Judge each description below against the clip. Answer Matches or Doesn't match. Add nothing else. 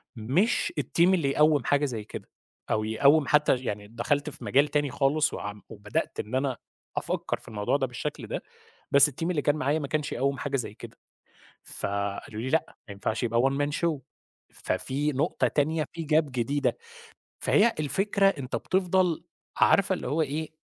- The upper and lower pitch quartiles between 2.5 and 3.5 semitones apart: Doesn't match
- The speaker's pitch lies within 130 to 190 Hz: Matches